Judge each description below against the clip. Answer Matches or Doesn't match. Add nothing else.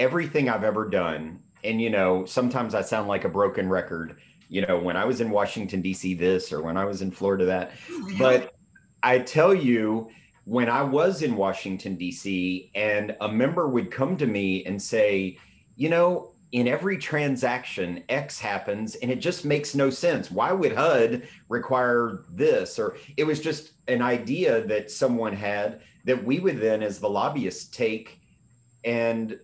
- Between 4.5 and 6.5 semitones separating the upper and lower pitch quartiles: Matches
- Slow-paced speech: Doesn't match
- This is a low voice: Matches